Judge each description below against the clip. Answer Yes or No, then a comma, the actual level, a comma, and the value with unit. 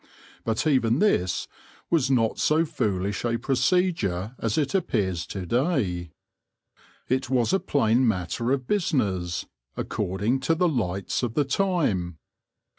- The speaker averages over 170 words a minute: No, slow, 135 wpm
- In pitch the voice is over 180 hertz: No, low, 120 Hz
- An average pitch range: No, wide, 7.2 semitones